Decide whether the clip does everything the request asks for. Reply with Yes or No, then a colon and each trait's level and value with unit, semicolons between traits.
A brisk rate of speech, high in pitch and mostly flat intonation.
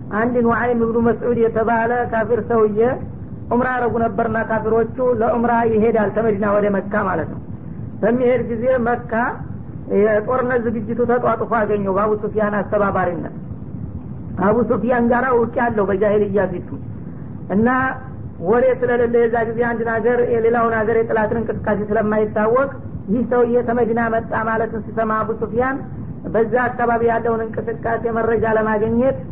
Yes: fast, 125 wpm; high, 230 Hz; narrow, 1.6 semitones